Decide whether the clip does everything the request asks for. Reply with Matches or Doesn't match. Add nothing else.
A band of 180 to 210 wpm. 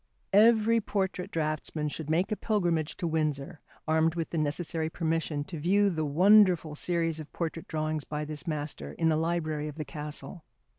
Doesn't match